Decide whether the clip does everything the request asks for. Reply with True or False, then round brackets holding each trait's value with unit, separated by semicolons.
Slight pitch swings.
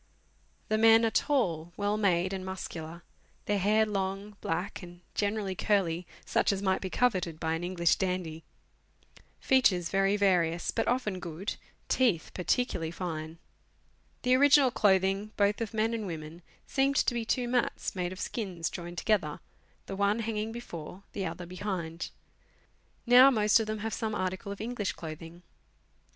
False (3.8 semitones)